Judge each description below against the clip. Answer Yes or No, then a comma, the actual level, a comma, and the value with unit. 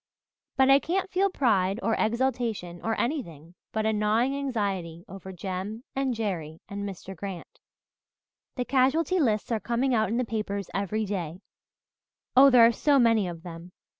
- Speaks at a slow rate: No, average, 165 wpm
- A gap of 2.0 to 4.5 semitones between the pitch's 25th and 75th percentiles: No, average, 5.1 semitones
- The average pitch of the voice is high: Yes, high, 220 Hz